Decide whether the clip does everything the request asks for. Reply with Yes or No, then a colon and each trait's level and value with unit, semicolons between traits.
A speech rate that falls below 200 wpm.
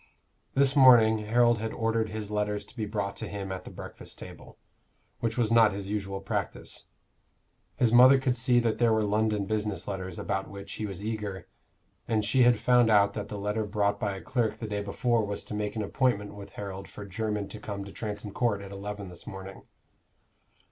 No: fast, 205 wpm